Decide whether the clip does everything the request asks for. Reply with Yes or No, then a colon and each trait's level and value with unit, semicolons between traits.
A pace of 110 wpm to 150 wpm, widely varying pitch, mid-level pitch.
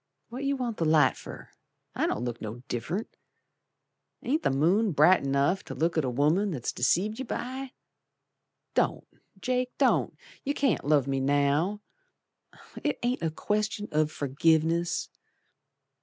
Yes: average, 145 wpm; wide, 7.7 semitones; medium, 165 Hz